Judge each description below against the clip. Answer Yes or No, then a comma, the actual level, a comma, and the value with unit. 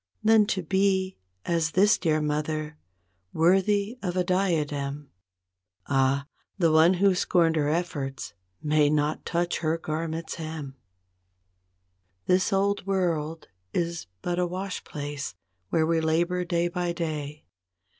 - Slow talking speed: Yes, slow, 130 wpm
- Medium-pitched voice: Yes, medium, 165 Hz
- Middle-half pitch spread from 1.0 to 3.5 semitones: Yes, average, 3.1 semitones